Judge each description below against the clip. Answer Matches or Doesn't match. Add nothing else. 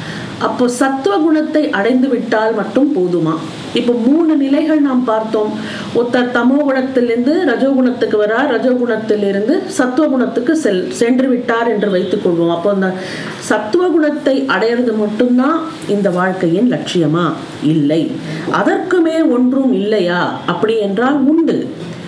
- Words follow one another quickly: Doesn't match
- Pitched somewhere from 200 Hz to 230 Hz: Doesn't match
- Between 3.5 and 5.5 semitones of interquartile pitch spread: Matches